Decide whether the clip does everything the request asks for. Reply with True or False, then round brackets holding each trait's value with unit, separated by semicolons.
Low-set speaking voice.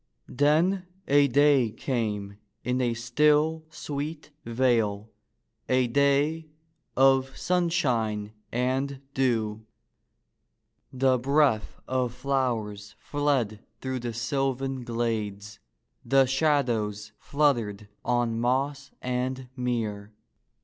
True (130 Hz)